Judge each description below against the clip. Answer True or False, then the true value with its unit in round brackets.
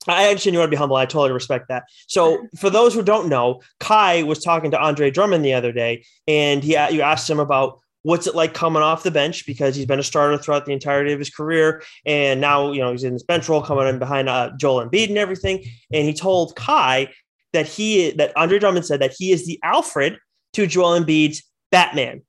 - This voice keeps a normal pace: False (230 wpm)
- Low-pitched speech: False (150 Hz)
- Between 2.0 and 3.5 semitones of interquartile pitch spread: False (4.0 semitones)